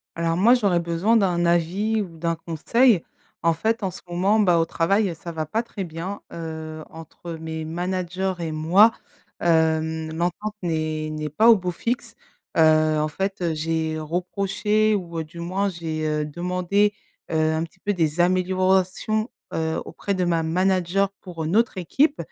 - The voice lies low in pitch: No, medium, 175 Hz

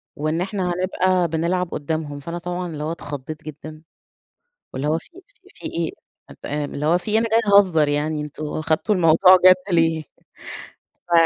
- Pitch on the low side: No, medium, 165 Hz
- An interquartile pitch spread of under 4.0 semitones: Yes, average, 3.0 semitones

